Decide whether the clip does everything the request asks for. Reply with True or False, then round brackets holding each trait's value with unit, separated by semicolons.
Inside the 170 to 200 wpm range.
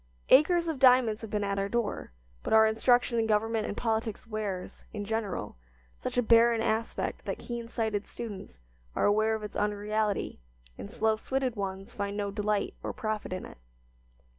True (175 wpm)